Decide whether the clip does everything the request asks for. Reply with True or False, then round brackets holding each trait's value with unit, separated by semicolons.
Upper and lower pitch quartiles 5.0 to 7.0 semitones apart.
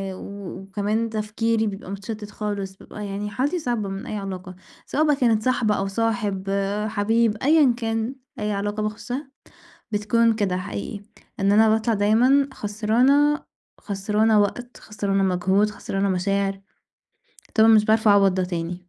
False (2.4 semitones)